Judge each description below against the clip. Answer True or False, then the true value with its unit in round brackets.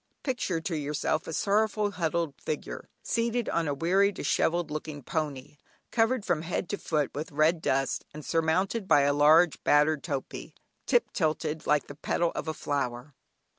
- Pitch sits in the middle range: True (160 Hz)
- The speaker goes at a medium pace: True (165 wpm)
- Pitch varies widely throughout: False (3.9 semitones)